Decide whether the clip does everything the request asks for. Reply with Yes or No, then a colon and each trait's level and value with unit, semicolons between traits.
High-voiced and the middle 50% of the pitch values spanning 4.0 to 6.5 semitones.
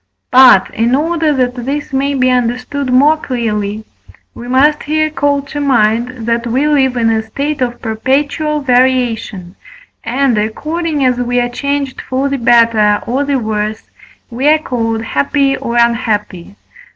No: very high, 250 Hz; average, 3.5 semitones